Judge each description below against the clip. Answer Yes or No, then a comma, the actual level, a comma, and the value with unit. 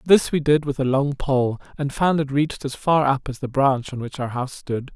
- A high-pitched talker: No, medium, 140 Hz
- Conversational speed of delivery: No, fast, 265 wpm